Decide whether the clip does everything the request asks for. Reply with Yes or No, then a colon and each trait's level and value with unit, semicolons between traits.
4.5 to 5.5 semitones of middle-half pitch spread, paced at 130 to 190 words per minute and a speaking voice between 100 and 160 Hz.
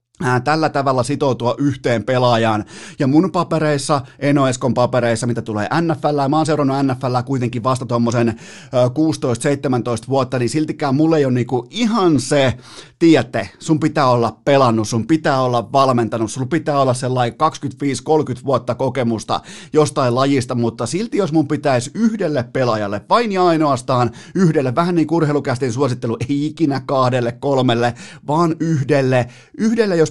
No: average, 3.8 semitones; average, 145 wpm; low, 135 Hz